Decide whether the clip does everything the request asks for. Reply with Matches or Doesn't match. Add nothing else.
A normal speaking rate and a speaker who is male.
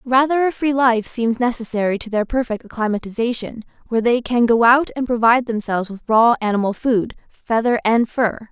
Doesn't match